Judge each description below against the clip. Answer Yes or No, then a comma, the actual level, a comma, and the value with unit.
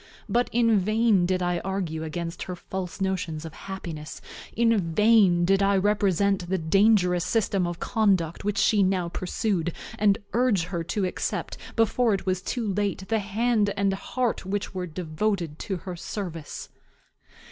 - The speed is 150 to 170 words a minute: Yes, average, 160 wpm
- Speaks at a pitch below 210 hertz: Yes, high, 190 Hz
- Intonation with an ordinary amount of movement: Yes, average, 3.0 semitones